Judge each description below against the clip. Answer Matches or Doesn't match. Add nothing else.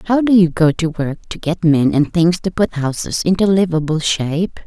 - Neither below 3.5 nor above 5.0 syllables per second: Matches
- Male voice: Doesn't match